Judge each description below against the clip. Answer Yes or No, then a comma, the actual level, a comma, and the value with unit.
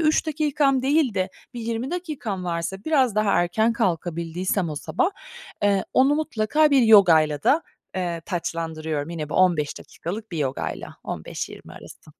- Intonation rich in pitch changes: Yes, wide, 8.0 semitones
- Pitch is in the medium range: No, high, 200 Hz